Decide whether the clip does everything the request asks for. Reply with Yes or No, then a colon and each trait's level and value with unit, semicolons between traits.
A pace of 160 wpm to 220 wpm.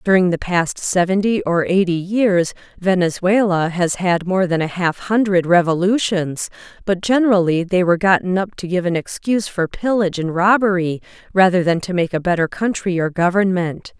Yes: average, 165 wpm